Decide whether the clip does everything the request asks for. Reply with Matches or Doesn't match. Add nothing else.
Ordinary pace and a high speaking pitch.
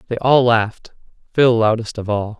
Doesn't match